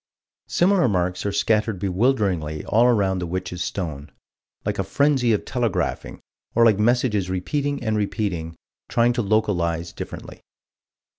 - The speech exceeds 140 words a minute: No, slow, 135 wpm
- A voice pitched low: Yes, low, 105 Hz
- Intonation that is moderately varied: Yes, average, 4.8 semitones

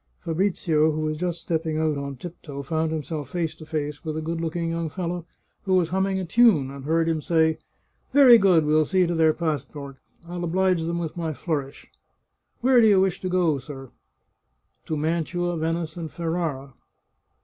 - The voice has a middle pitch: Yes, medium, 165 Hz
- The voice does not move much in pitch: Yes, narrow, 2.3 semitones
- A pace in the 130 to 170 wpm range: No, average, 195 wpm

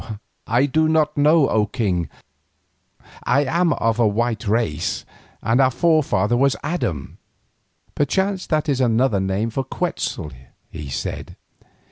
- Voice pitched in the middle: No, low, 125 Hz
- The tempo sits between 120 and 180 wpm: Yes, slow, 135 wpm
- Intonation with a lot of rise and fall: Yes, wide, 6.0 semitones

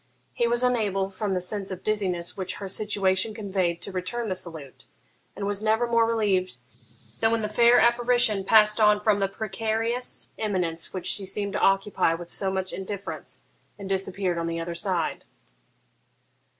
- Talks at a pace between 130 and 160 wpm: No, average, 170 wpm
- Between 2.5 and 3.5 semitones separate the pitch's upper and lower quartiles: Yes, average, 2.8 semitones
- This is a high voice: Yes, high, 200 Hz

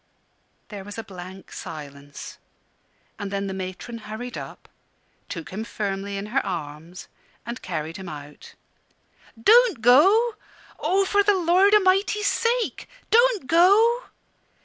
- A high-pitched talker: Yes, high, 225 Hz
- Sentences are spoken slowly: Yes, slow, 125 wpm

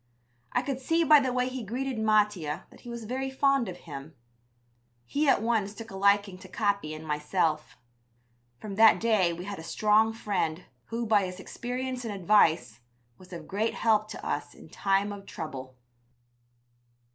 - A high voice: Yes, high, 205 Hz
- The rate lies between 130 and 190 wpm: Yes, average, 175 wpm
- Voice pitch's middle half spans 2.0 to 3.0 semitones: No, average, 4.5 semitones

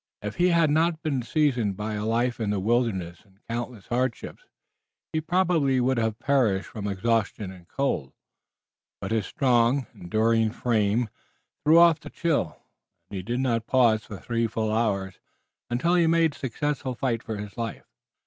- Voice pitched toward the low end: Yes, low, 115 Hz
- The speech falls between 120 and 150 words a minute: No, average, 170 wpm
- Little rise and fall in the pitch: No, average, 4.6 semitones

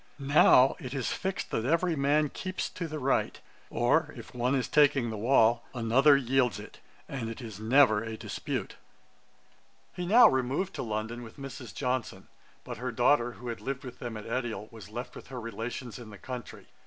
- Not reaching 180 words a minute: No, average, 190 wpm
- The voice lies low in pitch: Yes, low, 125 Hz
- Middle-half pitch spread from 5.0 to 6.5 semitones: No, average, 3.1 semitones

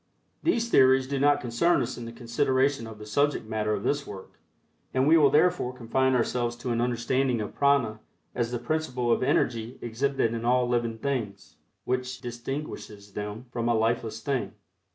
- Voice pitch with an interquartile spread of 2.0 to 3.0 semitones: Yes, average, 2.7 semitones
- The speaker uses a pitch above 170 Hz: No, low, 120 Hz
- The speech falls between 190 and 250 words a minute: No, average, 175 wpm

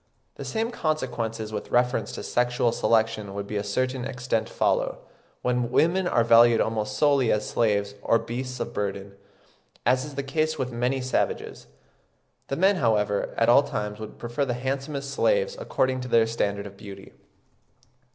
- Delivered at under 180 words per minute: Yes, average, 165 wpm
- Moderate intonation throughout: Yes, average, 4.0 semitones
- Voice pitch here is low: Yes, low, 120 Hz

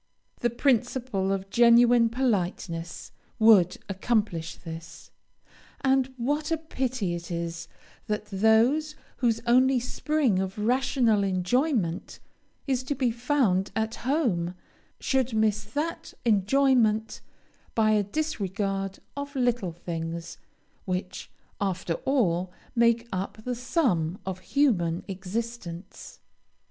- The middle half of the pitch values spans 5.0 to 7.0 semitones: Yes, average, 5.3 semitones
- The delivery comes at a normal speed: No, slow, 110 wpm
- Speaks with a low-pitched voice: No, high, 220 Hz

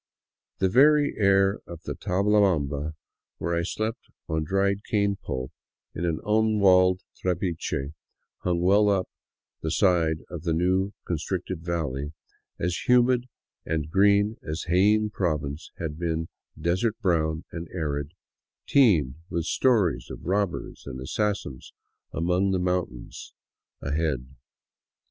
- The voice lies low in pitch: Yes, very low, 90 Hz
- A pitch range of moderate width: Yes, average, 4.1 semitones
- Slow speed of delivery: Yes, slow, 125 wpm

